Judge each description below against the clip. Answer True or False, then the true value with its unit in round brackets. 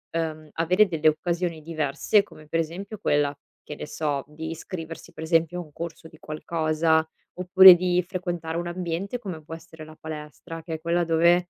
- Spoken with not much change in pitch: True (2.0 semitones)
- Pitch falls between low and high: True (165 Hz)